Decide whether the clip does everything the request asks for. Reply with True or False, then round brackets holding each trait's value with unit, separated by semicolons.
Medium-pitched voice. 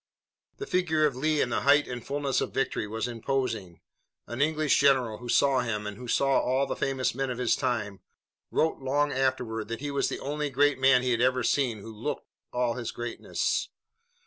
False (130 Hz)